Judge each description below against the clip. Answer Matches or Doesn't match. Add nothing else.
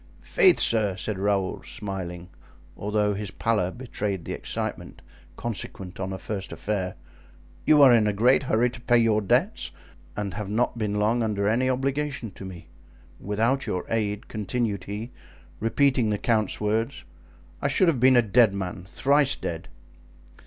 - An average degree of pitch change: Matches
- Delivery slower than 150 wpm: Doesn't match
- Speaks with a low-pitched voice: Matches